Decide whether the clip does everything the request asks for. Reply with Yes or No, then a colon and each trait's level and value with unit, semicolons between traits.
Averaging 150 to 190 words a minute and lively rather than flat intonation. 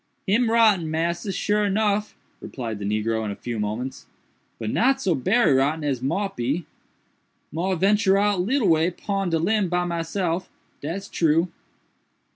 Yes: average, 155 wpm; wide, 6.0 semitones